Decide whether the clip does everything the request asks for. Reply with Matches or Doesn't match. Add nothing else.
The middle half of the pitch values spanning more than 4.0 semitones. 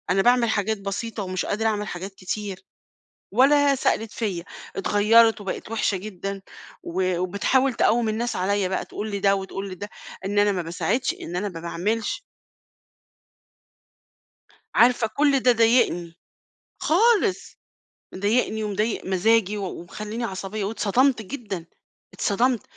Doesn't match